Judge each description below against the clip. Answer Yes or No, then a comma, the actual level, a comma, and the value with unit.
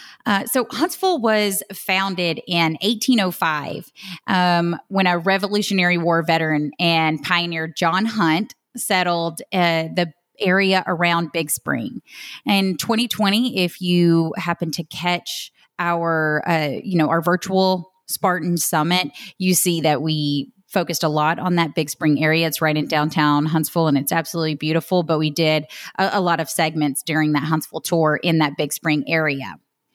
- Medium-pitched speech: Yes, medium, 170 Hz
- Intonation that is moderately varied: Yes, average, 3.0 semitones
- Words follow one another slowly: No, average, 155 wpm